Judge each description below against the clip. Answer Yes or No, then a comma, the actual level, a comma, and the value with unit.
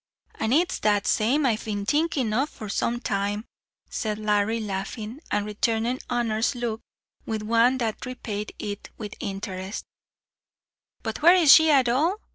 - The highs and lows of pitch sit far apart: No, average, 3.3 semitones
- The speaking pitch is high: Yes, high, 225 Hz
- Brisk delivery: No, average, 150 wpm